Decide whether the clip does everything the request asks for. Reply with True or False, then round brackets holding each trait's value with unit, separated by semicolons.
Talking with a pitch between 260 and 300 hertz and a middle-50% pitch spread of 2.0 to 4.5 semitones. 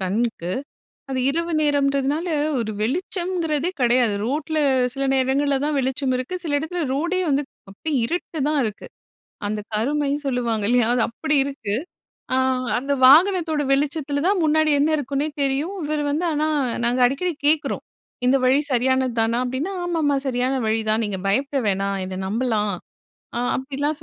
True (275 Hz; 3.9 semitones)